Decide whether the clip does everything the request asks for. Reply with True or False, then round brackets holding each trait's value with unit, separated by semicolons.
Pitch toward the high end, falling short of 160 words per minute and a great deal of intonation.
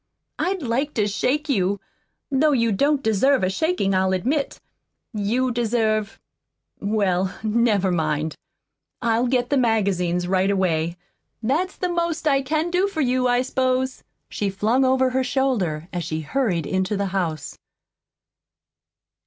True (230 Hz; 140 wpm; 5.9 semitones)